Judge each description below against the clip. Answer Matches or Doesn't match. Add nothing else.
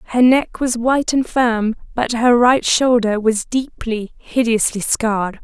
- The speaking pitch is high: Matches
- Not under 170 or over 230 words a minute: Doesn't match